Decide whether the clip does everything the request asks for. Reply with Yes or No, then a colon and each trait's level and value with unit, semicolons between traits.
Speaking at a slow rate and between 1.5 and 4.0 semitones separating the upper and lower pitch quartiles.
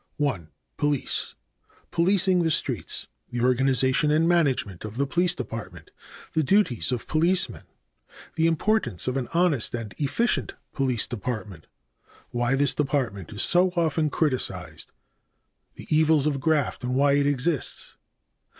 No: slow, 130 wpm; average, 4.8 semitones